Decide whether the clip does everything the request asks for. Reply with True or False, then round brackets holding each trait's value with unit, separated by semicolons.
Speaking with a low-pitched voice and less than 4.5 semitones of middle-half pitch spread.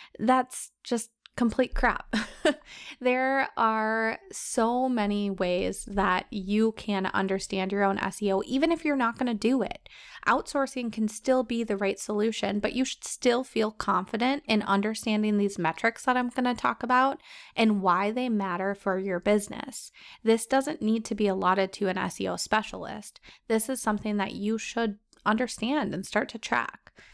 False (225 Hz; 3.8 semitones)